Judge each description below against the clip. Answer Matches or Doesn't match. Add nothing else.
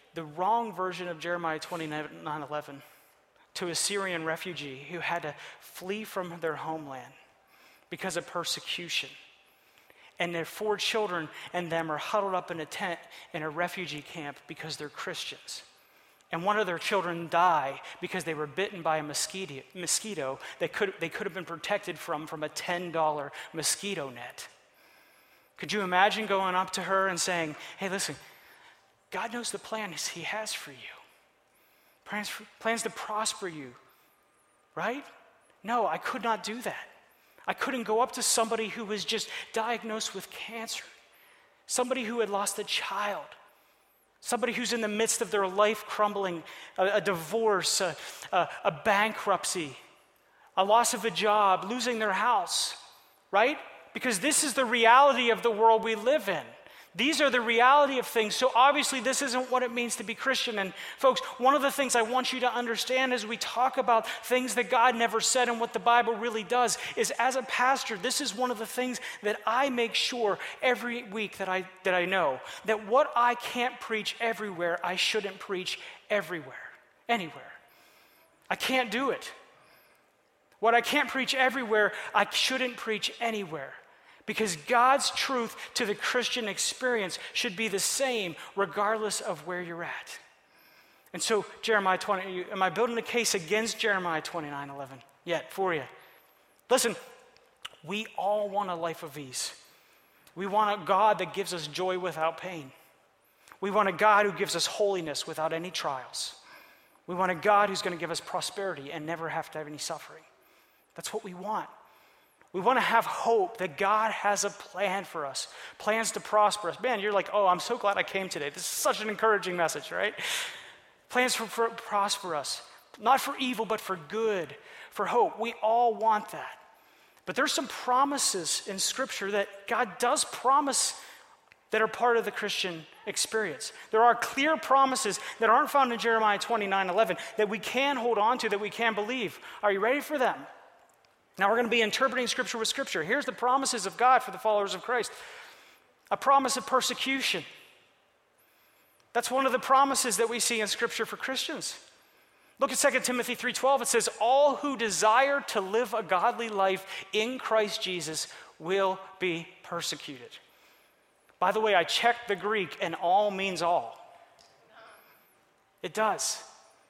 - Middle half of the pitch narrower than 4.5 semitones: Doesn't match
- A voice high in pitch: Matches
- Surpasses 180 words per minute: Doesn't match